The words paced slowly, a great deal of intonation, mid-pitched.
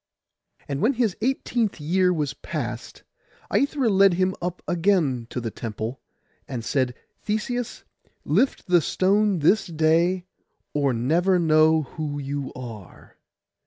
Yes: slow, 125 wpm; wide, 5.9 semitones; medium, 165 Hz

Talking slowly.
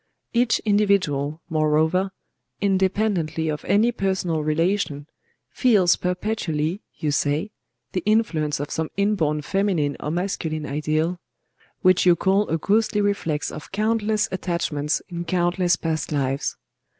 Yes: slow, 120 wpm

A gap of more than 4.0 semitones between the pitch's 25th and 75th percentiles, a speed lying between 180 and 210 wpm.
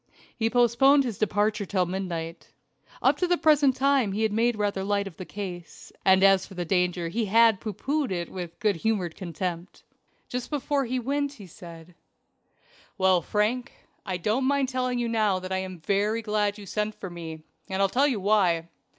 Yes: average, 4.6 semitones; average, 190 wpm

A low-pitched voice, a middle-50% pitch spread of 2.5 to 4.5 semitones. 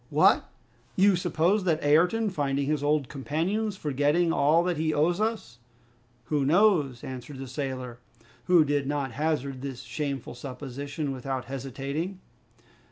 No: medium, 145 Hz; average, 3.9 semitones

